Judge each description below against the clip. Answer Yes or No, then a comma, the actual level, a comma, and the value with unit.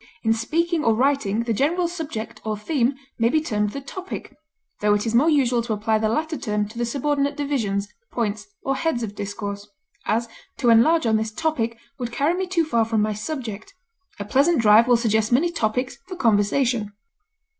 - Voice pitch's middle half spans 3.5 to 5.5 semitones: Yes, average, 5.0 semitones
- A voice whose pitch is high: Yes, high, 235 Hz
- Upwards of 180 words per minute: Yes, average, 190 wpm